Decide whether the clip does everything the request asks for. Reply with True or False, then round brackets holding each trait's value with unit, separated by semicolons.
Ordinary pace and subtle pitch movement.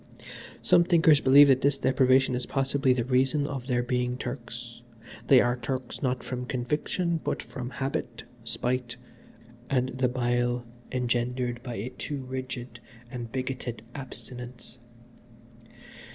False (130 wpm; 1.6 semitones)